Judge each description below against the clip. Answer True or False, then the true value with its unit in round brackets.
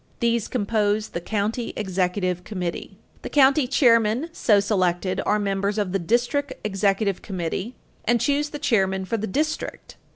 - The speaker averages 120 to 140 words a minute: False (150 wpm)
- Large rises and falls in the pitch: False (3.8 semitones)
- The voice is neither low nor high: False (210 Hz)